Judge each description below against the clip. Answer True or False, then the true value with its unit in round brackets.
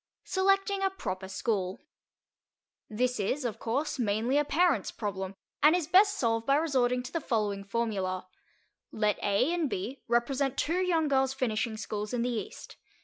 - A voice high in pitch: True (245 Hz)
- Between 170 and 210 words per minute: False (160 wpm)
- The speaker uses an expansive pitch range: True (5.9 semitones)